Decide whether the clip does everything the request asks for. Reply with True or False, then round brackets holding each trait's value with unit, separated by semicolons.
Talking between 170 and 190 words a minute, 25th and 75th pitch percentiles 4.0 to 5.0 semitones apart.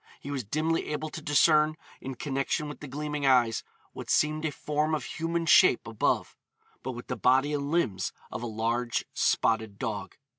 True (180 wpm; 4.3 semitones)